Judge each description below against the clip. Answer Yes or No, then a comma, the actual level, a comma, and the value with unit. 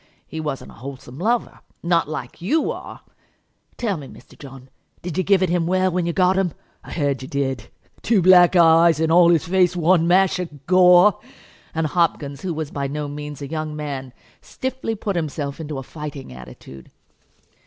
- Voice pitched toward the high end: No, medium, 165 Hz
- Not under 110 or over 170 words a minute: No, average, 185 wpm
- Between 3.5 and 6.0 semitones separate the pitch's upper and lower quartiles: Yes, average, 4.2 semitones